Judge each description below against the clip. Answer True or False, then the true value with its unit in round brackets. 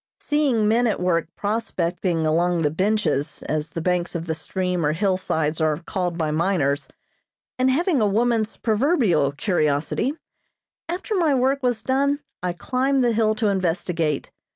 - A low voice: False (185 Hz)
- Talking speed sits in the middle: True (155 wpm)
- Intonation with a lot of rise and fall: True (6.8 semitones)